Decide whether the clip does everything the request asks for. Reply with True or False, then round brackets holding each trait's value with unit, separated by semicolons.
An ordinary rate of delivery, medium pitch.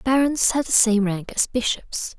False (190 wpm; 235 Hz)